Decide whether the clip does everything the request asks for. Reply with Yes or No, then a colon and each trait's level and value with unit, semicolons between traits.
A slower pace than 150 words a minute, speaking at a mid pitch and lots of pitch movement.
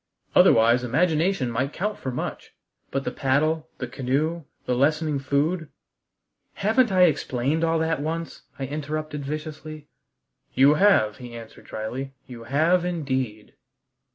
No: slow, 135 wpm; medium, 150 Hz; average, 3.8 semitones